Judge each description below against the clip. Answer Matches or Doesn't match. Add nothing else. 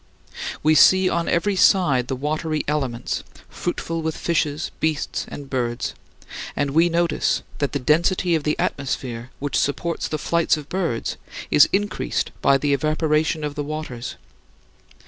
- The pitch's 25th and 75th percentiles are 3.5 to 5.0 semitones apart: Doesn't match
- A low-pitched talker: Doesn't match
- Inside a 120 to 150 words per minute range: Matches